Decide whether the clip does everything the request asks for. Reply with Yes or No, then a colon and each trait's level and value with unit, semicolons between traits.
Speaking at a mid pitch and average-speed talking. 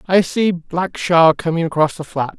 Yes: medium, 170 Hz; average, 175 wpm